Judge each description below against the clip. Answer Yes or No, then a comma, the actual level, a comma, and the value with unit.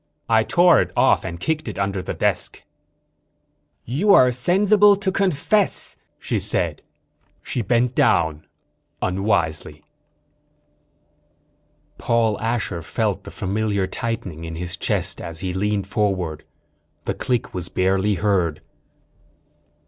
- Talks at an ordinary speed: No, slow, 120 wpm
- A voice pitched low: Yes, low, 100 Hz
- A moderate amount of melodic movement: No, wide, 5.7 semitones